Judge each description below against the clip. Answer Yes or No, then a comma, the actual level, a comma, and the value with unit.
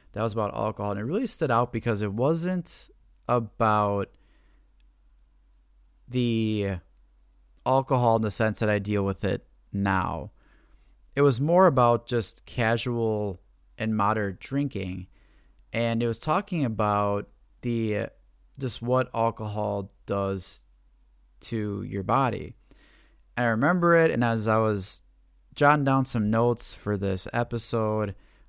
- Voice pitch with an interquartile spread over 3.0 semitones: Yes, average, 3.4 semitones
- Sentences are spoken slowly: Yes, slow, 130 wpm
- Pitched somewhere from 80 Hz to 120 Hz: Yes, low, 110 Hz